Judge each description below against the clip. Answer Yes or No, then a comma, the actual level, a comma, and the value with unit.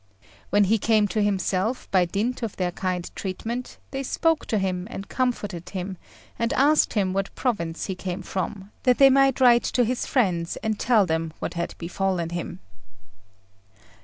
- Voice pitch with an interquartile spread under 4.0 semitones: No, average, 4.8 semitones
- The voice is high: Yes, high, 200 Hz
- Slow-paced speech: No, average, 170 wpm